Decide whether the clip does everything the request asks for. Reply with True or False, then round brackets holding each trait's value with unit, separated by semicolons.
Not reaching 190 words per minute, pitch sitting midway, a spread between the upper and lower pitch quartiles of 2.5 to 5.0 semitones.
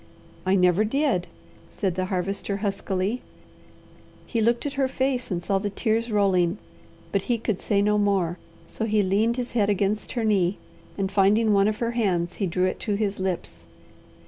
False (180 wpm; 200 Hz; 2.9 semitones)